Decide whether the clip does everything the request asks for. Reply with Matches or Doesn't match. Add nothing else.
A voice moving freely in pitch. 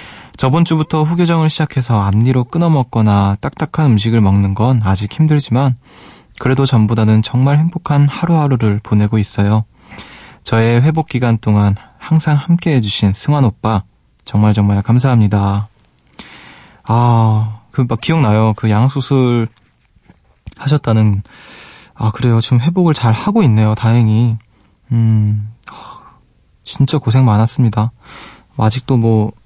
Doesn't match